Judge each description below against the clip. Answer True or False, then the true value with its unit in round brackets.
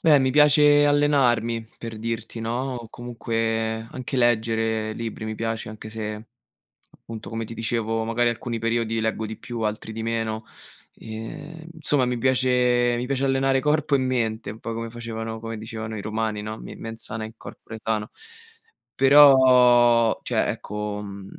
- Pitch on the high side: False (115 Hz)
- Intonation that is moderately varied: False (2.1 semitones)